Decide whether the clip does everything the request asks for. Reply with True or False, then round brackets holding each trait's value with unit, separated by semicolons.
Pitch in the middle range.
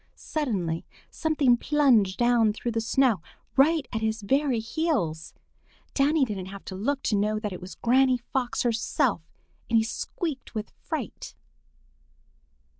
False (235 Hz)